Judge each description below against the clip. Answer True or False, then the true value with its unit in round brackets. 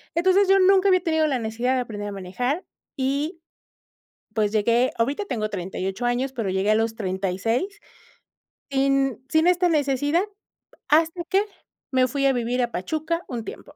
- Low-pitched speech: False (260 Hz)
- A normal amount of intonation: False (6.2 semitones)